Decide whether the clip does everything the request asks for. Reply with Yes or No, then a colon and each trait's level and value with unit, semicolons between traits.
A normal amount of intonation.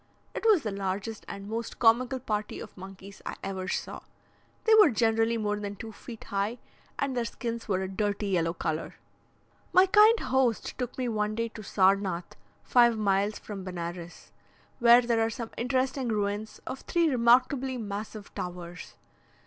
Yes: average, 3.7 semitones